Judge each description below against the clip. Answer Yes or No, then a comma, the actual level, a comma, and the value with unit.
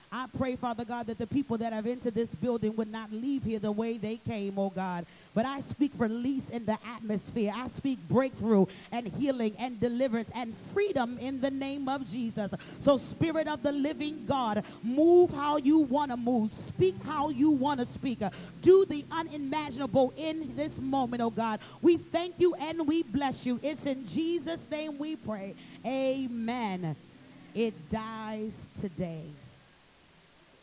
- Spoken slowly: No, average, 170 wpm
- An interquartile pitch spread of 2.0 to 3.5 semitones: No, average, 4.7 semitones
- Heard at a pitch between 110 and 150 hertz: No, high, 245 Hz